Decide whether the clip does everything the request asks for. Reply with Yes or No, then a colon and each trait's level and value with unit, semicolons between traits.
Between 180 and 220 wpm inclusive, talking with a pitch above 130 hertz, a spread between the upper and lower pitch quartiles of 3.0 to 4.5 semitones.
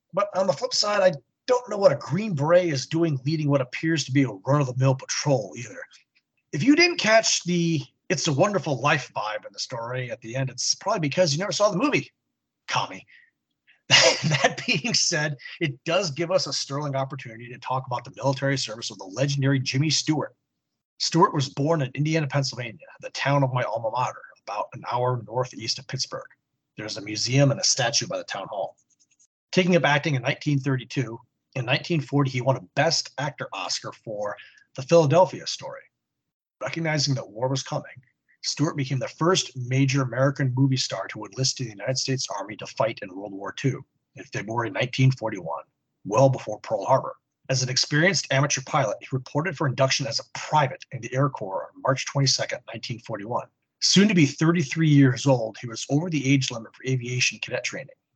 Yes: average, 190 wpm; medium, 140 Hz; average, 3.6 semitones